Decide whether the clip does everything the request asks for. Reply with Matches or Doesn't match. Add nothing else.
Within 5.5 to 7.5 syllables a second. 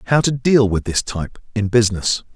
Matches